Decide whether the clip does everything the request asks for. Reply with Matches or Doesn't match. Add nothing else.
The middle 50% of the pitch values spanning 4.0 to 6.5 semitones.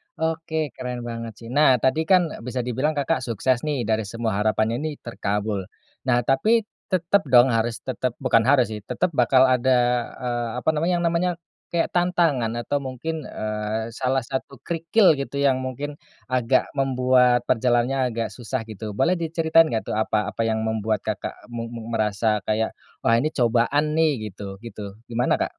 Matches